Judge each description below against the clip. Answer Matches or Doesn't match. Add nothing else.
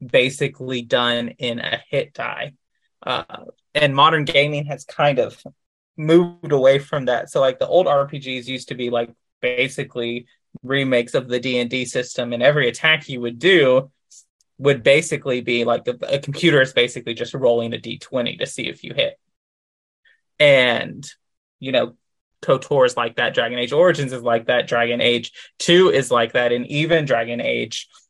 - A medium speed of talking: Matches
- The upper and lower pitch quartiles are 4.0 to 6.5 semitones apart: Doesn't match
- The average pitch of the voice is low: Matches